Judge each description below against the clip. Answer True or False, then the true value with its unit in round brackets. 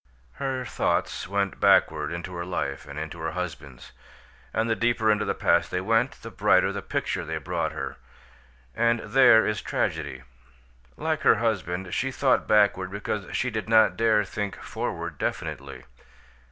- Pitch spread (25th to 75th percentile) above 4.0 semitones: True (4.4 semitones)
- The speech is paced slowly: False (160 wpm)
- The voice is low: True (100 Hz)